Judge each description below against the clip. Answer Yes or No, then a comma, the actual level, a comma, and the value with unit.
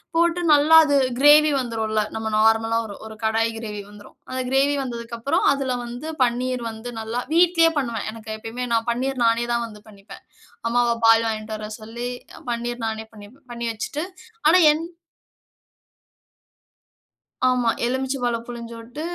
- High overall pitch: Yes, high, 235 Hz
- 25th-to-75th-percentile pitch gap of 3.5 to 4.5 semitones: No, average, 2.7 semitones